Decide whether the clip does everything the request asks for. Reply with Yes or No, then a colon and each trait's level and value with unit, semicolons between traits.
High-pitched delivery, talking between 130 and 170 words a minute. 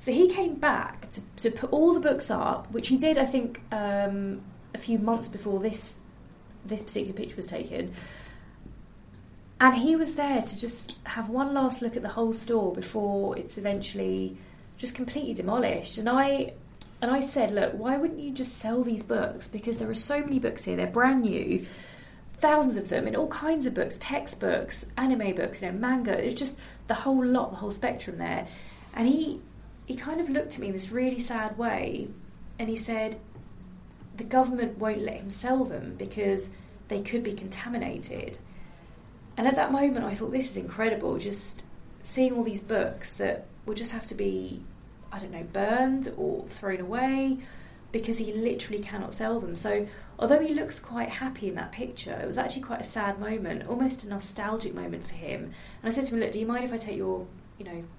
No: high, 230 Hz; average, 200 wpm